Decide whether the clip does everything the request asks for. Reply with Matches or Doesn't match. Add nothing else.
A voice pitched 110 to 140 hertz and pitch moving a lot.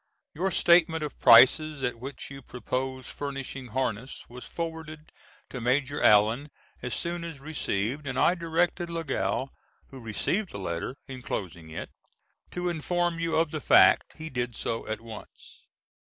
Doesn't match